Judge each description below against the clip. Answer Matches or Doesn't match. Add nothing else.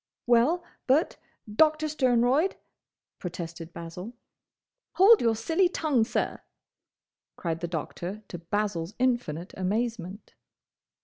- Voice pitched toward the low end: Doesn't match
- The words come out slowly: Matches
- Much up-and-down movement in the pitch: Matches